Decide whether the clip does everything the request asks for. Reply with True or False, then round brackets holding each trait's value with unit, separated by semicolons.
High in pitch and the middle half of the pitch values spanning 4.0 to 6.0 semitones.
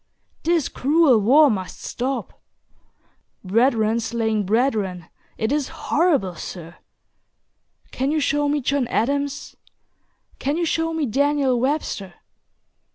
True (265 Hz; 5.0 semitones)